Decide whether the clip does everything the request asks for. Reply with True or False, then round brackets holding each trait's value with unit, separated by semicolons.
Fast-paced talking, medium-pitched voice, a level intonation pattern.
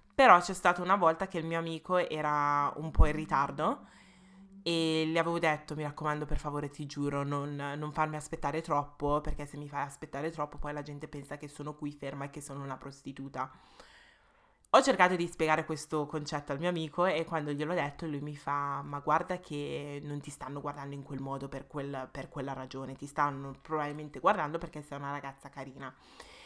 True (200 wpm; 150 Hz; 2.2 semitones)